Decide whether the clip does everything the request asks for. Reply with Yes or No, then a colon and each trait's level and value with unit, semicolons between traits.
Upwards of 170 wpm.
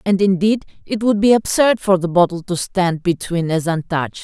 Yes: average, 200 wpm